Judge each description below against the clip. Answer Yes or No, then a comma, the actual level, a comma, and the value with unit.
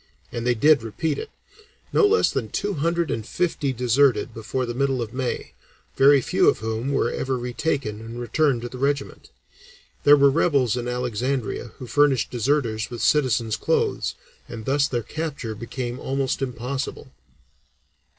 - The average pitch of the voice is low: Yes, low, 130 Hz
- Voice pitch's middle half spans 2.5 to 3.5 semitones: Yes, average, 3.1 semitones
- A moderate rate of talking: Yes, average, 160 wpm